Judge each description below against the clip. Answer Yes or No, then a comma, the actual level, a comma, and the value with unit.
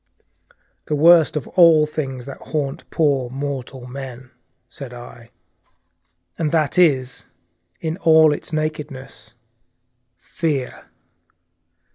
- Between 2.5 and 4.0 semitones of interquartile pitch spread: Yes, average, 3.2 semitones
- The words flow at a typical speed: No, slow, 105 wpm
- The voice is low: No, medium, 145 Hz